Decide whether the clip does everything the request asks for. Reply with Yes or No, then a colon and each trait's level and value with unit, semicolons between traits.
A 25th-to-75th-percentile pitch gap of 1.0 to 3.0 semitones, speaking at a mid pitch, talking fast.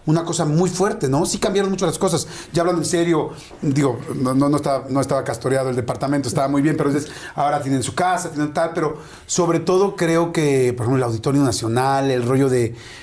No: average, 4.1 semitones; medium, 145 Hz; fast, 215 wpm